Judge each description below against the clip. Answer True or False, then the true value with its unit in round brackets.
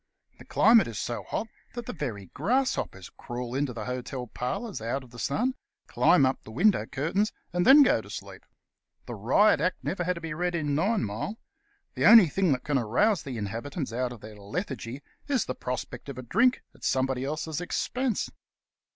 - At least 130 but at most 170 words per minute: False (190 wpm)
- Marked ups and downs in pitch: True (7.8 semitones)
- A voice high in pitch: False (145 Hz)